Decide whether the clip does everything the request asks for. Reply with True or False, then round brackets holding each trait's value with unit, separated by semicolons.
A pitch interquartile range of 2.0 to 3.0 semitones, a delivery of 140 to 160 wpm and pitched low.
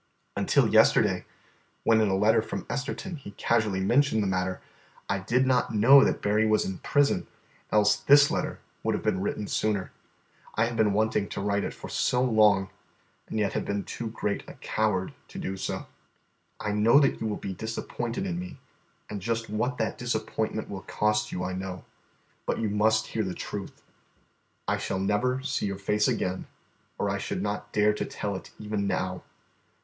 False (2.6 semitones; 185 wpm; 105 Hz)